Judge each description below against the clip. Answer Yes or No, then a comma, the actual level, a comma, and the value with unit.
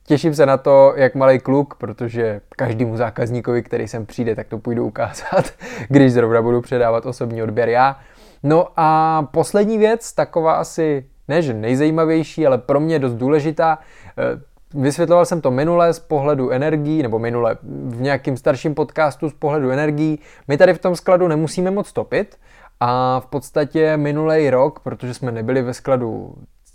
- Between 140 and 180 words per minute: Yes, average, 160 wpm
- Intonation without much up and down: No, average, 4.4 semitones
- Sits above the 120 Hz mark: Yes, medium, 140 Hz